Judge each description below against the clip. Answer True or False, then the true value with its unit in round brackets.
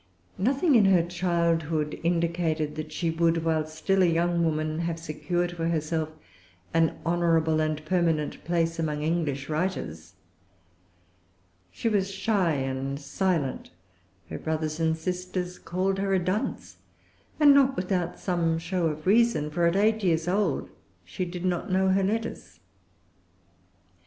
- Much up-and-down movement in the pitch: False (2.9 semitones)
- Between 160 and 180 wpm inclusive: False (140 wpm)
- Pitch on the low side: False (170 Hz)